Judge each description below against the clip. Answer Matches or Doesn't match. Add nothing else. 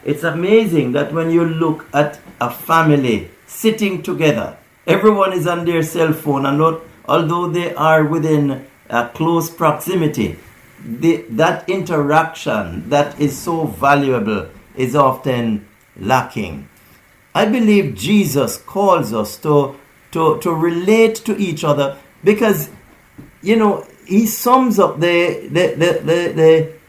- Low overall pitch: Doesn't match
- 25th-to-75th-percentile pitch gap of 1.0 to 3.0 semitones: Doesn't match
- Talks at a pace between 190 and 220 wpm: Doesn't match